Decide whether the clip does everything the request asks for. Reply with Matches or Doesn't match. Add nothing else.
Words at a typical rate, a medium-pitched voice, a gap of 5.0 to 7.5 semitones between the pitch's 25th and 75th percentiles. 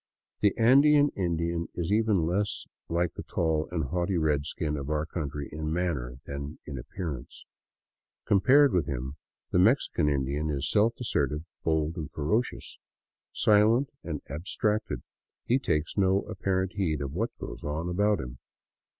Doesn't match